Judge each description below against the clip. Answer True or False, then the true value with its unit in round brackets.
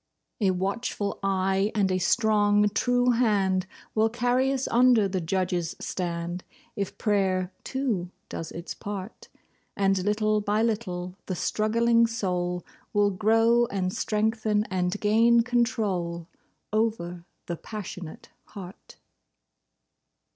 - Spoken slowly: True (115 wpm)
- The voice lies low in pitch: False (205 Hz)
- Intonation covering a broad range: False (3.4 semitones)